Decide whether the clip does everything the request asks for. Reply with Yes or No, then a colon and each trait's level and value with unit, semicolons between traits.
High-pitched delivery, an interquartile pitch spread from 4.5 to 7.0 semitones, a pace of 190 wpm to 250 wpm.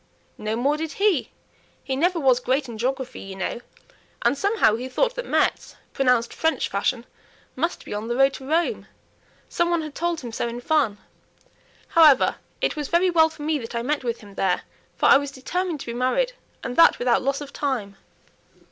Yes: very high, 270 Hz; average, 5.1 semitones; average, 200 wpm